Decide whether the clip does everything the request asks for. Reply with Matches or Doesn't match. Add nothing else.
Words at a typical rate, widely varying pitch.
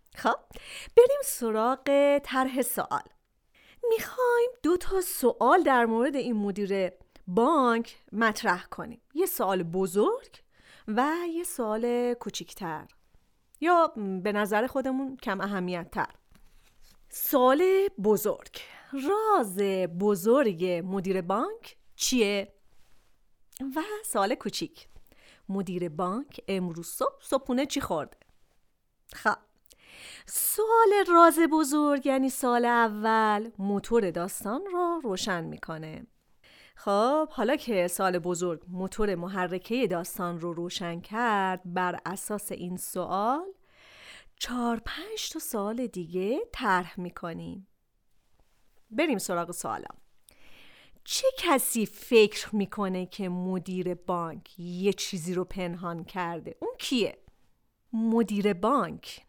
Doesn't match